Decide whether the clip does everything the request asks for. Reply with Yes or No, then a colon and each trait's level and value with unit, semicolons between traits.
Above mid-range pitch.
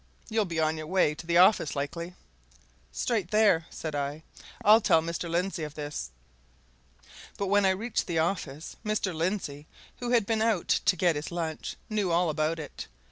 No: medium, 170 Hz